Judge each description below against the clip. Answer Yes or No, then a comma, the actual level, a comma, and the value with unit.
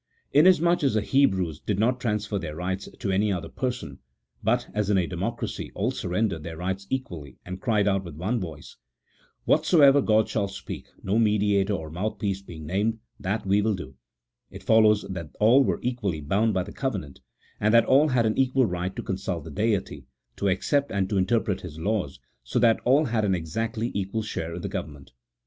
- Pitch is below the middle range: Yes, low, 100 Hz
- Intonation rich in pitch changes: No, average, 3.8 semitones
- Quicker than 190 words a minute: Yes, average, 200 wpm